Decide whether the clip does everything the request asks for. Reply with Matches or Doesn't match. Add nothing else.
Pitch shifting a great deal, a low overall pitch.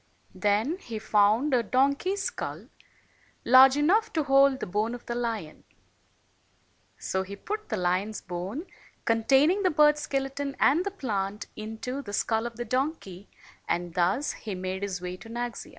Doesn't match